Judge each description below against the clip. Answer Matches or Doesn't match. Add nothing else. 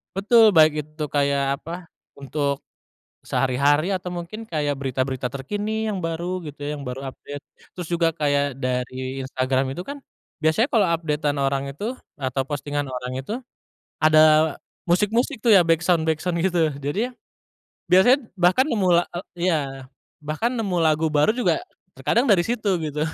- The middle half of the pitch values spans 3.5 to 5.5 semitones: Matches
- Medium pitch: Matches